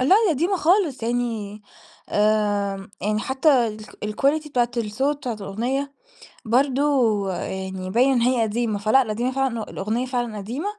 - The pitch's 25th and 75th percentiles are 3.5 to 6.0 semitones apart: Yes, average, 4.0 semitones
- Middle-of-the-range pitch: No, high, 235 Hz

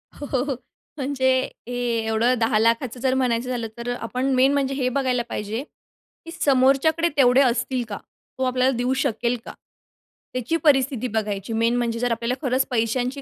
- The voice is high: Yes, very high, 250 Hz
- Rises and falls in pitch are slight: Yes, narrow, 2.3 semitones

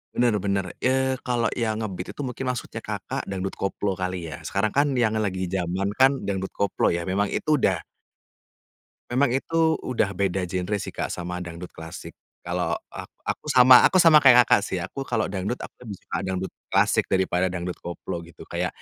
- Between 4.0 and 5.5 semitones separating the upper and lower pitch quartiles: Yes, average, 5.0 semitones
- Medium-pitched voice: No, low, 100 Hz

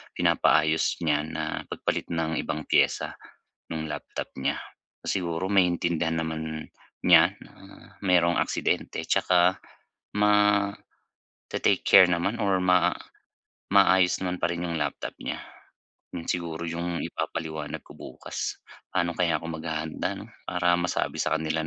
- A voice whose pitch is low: Yes, very low, 85 Hz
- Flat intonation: Yes, narrow, 2.3 semitones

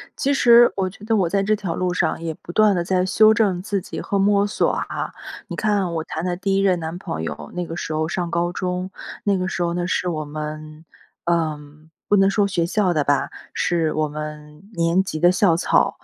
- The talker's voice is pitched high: No, medium, 175 Hz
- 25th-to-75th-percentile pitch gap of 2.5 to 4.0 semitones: Yes, average, 3.4 semitones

